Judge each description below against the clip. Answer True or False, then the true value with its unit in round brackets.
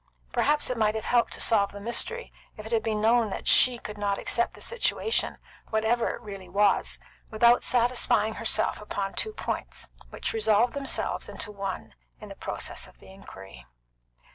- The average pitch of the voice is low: False (220 Hz)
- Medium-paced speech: True (170 wpm)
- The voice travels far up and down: False (3.0 semitones)